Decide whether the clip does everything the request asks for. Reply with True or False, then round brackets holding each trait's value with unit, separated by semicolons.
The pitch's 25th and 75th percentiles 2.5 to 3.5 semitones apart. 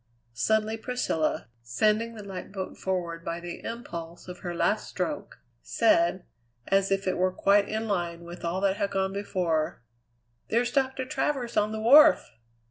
False (4.3 semitones)